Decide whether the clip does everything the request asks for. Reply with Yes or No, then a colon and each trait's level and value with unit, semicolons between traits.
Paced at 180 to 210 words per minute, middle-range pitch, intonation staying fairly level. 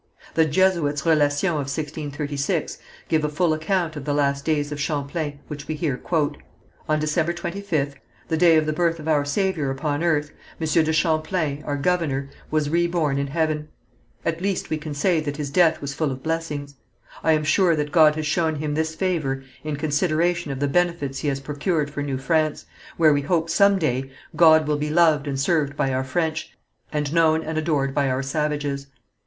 Yes: average, 195 wpm; medium, 155 Hz; narrow, 2.2 semitones